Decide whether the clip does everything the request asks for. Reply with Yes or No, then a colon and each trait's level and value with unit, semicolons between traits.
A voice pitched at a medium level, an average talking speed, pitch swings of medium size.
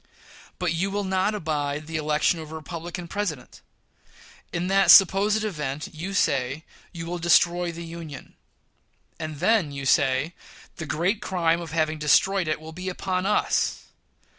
Yes: medium, 170 Hz; average, 155 wpm; average, 3.3 semitones